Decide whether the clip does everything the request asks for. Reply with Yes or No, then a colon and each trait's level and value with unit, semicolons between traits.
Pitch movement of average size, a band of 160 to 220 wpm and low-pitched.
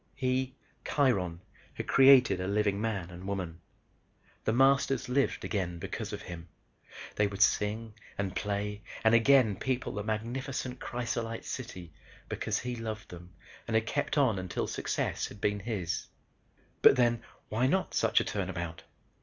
No: average, 4.5 semitones; average, 150 wpm; low, 110 Hz